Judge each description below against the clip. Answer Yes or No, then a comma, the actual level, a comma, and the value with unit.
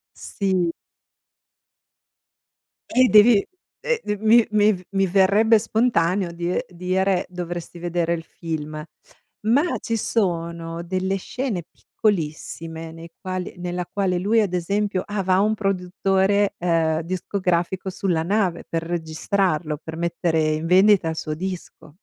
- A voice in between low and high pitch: Yes, medium, 180 Hz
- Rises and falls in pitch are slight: No, average, 3.2 semitones